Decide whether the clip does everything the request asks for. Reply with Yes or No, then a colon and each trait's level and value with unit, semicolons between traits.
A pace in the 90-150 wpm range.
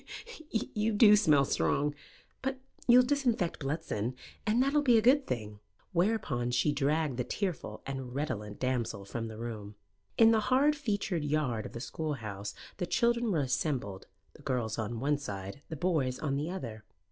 No: average, 170 wpm